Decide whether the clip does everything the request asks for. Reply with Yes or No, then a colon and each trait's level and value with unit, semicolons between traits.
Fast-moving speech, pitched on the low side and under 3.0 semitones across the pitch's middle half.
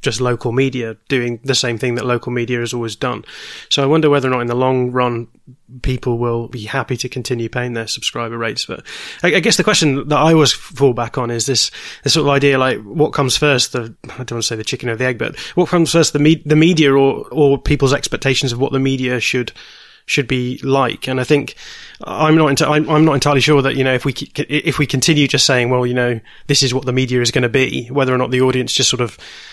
Yes: fast, 255 wpm; low, 130 Hz; narrow, 2.6 semitones